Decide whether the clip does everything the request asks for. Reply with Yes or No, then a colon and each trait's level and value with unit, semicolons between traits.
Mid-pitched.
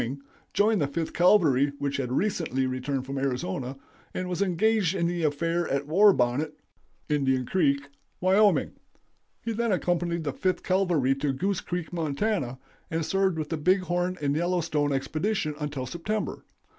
Yes: medium, 165 Hz